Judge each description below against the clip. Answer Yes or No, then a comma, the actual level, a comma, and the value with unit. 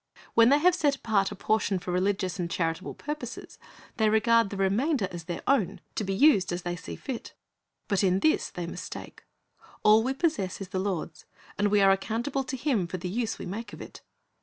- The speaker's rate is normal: No, fast, 210 wpm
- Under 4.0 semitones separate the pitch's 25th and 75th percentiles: No, average, 4.8 semitones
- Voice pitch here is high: Yes, high, 205 Hz